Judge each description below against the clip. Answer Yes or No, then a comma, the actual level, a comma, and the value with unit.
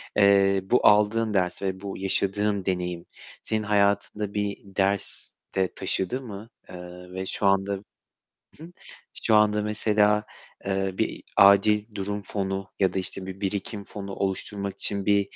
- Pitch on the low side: Yes, low, 100 Hz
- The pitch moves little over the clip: Yes, narrow, 1.4 semitones